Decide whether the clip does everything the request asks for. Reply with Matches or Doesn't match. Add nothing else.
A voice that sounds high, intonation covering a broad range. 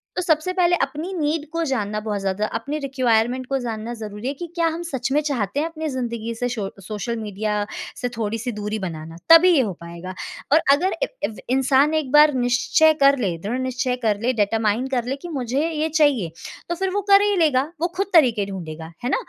Matches